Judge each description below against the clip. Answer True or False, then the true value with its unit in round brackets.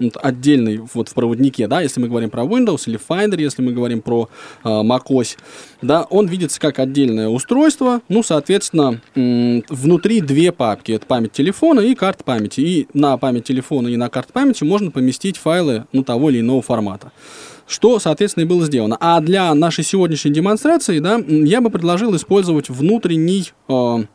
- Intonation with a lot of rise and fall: True (7.4 semitones)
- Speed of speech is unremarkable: False (170 wpm)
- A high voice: False (145 Hz)